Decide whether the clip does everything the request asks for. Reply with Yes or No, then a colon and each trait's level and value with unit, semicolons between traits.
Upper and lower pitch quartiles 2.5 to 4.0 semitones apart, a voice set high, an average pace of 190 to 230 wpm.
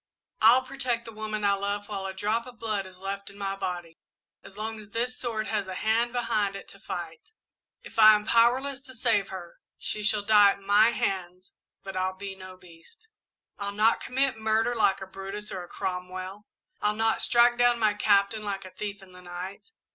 Yes: average, 2.8 semitones; high, 210 Hz; fast, 205 wpm